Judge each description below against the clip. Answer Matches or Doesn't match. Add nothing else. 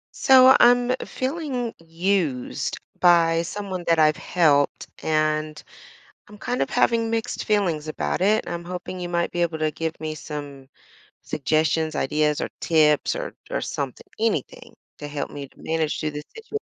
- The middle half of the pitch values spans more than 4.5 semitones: Matches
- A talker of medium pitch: Matches